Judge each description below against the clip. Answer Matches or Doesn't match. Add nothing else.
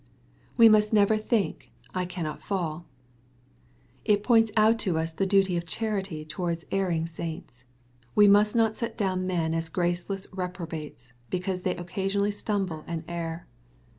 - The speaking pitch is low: Doesn't match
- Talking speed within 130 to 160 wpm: Matches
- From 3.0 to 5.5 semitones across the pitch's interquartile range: Matches